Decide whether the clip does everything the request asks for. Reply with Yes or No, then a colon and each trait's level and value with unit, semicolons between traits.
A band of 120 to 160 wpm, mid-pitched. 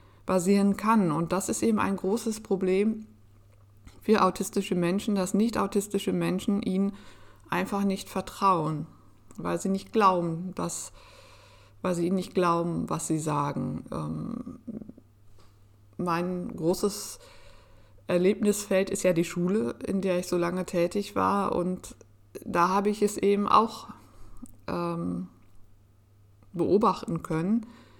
Yes: slow, 125 wpm; medium, 180 Hz